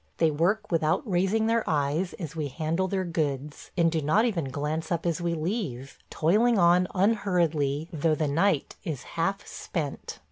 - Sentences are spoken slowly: No, average, 170 wpm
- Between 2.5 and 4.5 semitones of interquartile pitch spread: Yes, average, 3.8 semitones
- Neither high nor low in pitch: Yes, medium, 165 Hz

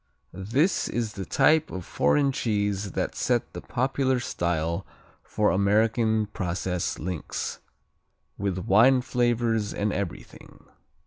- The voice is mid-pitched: No, low, 105 Hz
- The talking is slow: Yes, slow, 115 wpm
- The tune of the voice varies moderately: Yes, average, 4.3 semitones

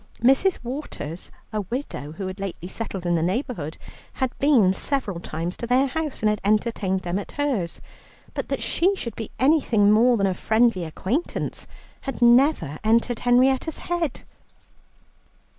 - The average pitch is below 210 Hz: No, high, 230 Hz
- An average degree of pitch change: No, wide, 6.0 semitones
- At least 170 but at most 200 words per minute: No, average, 155 wpm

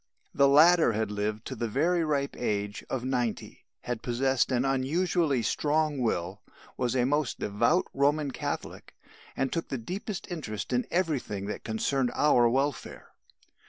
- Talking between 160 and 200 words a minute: No, average, 150 wpm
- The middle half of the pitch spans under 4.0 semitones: No, average, 4.5 semitones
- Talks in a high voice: No, low, 130 Hz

